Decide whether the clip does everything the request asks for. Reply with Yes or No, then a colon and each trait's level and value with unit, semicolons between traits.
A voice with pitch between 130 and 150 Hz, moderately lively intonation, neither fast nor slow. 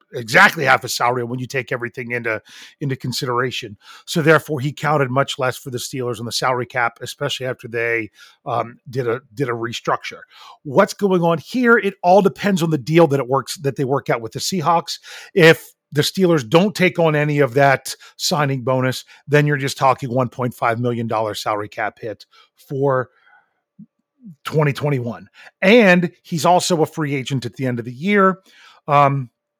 Yes: medium, 140 Hz; average, 5.0 semitones; average, 180 wpm